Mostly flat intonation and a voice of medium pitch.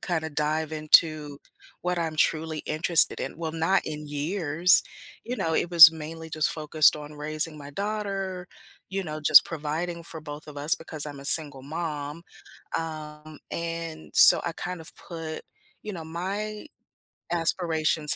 Yes: narrow, 1.9 semitones; medium, 160 Hz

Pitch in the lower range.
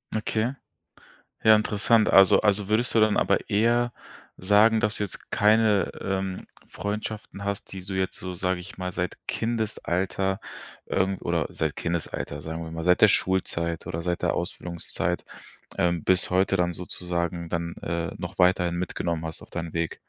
Yes: very low, 95 Hz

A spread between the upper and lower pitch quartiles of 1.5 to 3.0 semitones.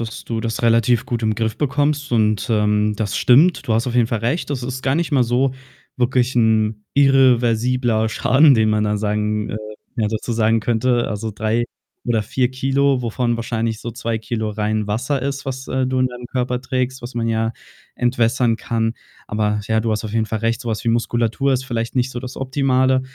Yes: average, 2.7 semitones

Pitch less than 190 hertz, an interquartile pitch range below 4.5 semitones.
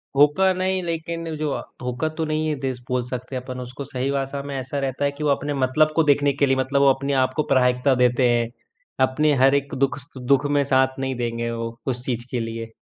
Yes: low, 135 Hz; narrow, 2.4 semitones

